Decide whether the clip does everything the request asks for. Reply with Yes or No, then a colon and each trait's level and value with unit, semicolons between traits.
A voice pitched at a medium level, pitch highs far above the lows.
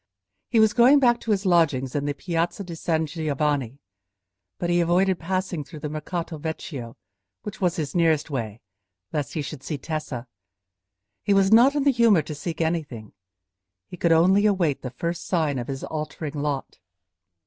No: medium, 165 Hz; average, 4.3 semitones